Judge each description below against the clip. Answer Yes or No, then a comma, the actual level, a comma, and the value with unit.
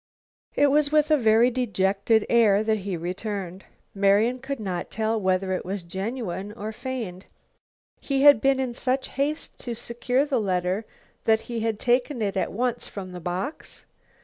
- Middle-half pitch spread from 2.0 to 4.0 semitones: No, average, 4.6 semitones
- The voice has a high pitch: Yes, high, 220 Hz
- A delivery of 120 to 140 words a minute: No, average, 170 wpm